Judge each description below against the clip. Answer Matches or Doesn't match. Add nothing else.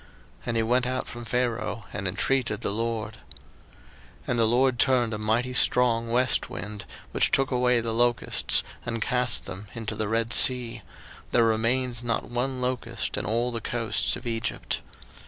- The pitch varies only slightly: Matches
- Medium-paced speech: Matches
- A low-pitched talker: Matches